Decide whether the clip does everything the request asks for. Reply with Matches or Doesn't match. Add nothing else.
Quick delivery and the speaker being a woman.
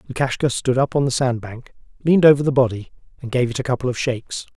Doesn't match